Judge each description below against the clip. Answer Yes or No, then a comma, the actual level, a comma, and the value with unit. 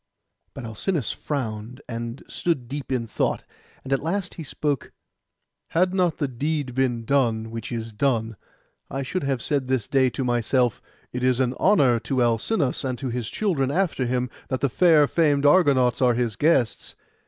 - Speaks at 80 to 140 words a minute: No, average, 175 wpm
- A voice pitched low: Yes, low, 130 Hz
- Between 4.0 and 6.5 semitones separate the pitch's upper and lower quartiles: No, average, 3.3 semitones